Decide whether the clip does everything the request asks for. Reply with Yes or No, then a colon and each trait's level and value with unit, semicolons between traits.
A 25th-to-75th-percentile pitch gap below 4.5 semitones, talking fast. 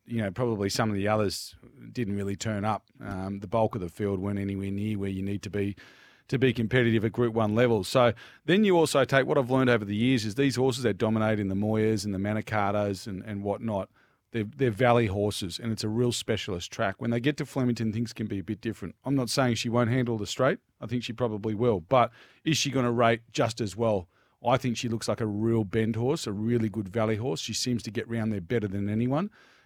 Yes: average, 3.0 semitones; fast, 250 wpm